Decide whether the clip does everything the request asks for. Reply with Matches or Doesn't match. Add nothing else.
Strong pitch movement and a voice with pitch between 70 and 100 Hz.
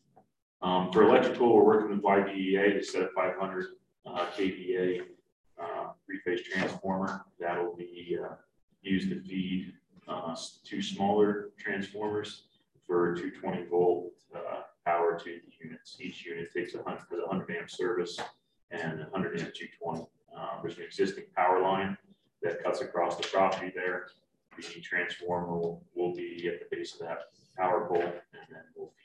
Doesn't match